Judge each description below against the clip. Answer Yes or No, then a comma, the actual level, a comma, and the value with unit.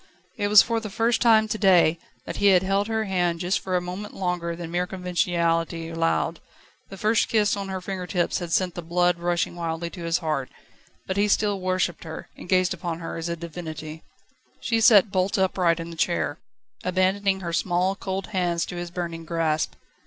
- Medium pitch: Yes, medium, 180 Hz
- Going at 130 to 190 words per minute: No, fast, 205 wpm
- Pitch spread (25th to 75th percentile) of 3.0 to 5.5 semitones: No, narrow, 2.4 semitones